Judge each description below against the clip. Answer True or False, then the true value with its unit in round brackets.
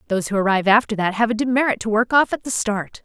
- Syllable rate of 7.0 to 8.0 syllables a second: True (7.1 syllables/s)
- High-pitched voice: True (220 Hz)